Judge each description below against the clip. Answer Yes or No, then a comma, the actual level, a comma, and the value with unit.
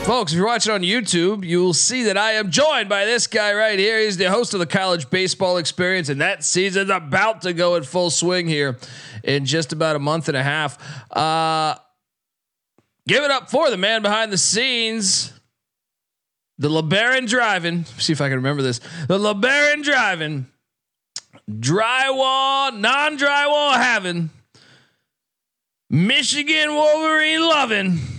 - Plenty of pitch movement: Yes, wide, 6.7 semitones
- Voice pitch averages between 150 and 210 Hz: Yes, medium, 185 Hz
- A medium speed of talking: Yes, average, 155 wpm